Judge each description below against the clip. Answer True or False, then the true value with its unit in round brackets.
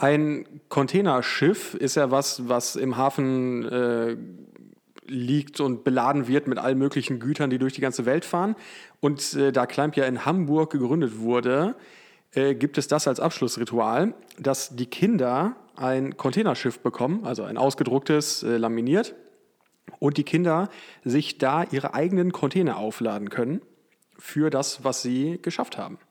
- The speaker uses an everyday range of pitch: True (3.3 semitones)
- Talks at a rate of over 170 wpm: False (150 wpm)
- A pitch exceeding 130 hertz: True (140 Hz)